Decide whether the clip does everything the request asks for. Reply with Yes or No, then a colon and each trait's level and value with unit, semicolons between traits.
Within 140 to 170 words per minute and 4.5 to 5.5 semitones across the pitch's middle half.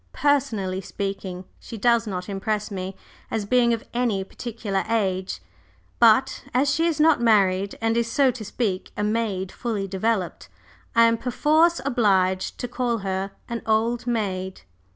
No: average, 150 wpm; average, 3.7 semitones